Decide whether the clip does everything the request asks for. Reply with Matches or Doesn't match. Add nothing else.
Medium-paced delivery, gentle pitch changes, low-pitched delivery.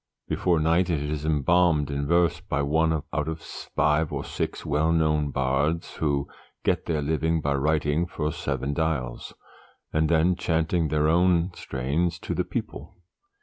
Matches